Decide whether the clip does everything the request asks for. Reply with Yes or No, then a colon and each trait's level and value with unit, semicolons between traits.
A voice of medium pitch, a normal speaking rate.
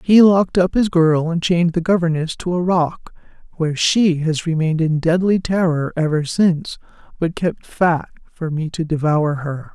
Yes: medium, 165 Hz; average, 180 wpm